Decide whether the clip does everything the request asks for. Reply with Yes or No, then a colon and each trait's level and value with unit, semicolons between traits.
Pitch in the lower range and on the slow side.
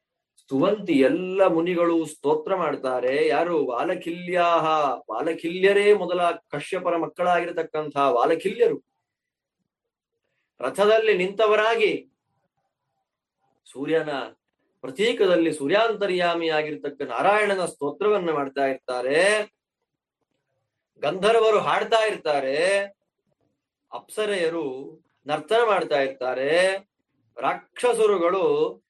No: medium, 180 Hz; slow, 60 wpm